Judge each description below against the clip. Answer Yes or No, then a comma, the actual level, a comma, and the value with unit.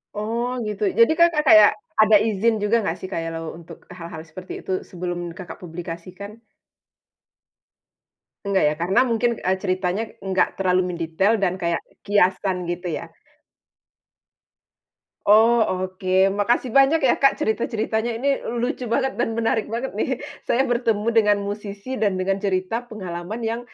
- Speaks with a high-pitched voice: Yes, high, 205 Hz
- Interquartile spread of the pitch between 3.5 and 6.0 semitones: Yes, average, 3.9 semitones